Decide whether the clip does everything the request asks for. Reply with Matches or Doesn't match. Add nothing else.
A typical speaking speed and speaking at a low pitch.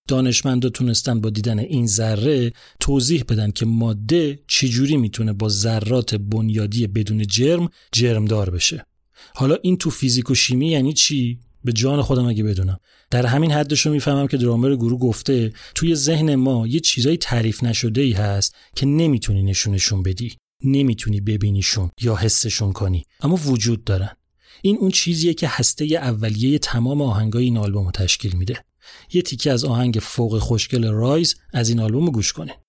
Doesn't match